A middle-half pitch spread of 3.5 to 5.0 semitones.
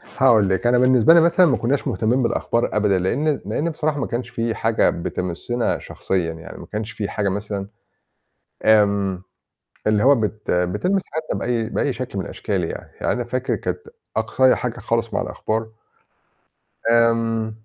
Yes: average, 3.9 semitones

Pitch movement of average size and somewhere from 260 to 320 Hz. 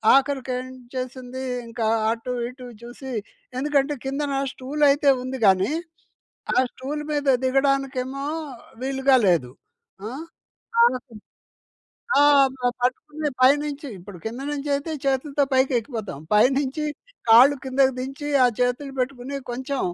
No: narrow, 2.0 semitones; very high, 265 Hz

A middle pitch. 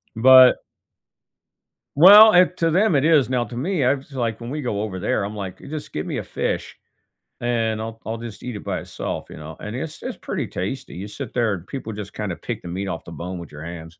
No: low, 115 Hz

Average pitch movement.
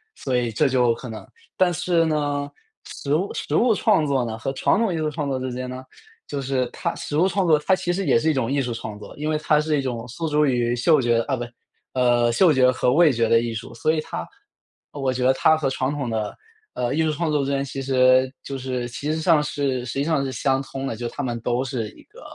Yes: average, 3.7 semitones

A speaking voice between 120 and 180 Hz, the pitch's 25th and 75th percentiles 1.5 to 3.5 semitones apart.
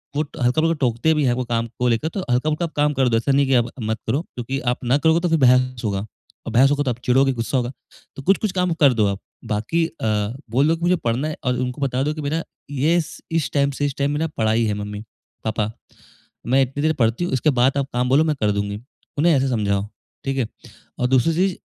No: low, 135 Hz; average, 4.5 semitones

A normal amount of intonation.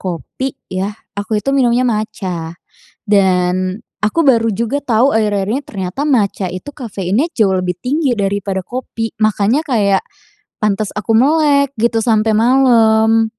Yes: average, 4.2 semitones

